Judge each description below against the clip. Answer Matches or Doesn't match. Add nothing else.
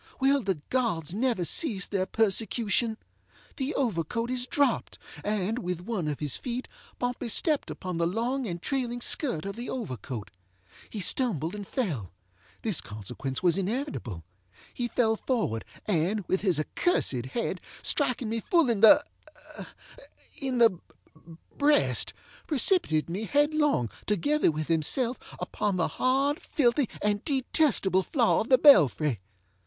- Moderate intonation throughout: Doesn't match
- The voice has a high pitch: Matches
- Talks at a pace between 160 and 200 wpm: Doesn't match